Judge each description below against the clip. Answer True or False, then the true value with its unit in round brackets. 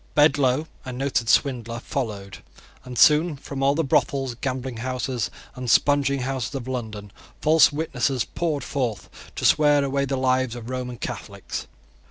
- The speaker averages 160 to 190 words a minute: False (150 wpm)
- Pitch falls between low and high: False (130 Hz)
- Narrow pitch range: True (2.3 semitones)